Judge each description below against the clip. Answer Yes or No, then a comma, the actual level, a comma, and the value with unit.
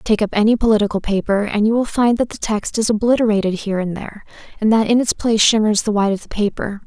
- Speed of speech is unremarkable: No, fast, 245 wpm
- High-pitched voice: Yes, high, 215 Hz